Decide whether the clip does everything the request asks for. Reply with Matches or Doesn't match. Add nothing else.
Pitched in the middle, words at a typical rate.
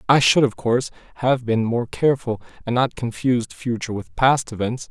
Doesn't match